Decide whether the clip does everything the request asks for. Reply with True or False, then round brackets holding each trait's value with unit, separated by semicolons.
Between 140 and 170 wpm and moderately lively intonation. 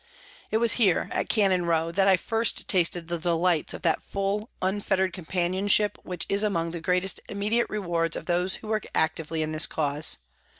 False (180 wpm; 3.2 semitones)